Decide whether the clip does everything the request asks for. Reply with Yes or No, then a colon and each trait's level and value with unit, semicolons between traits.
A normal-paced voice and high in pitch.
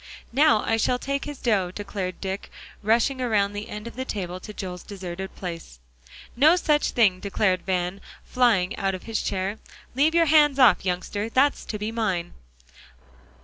Yes: average, 170 wpm; high, 210 Hz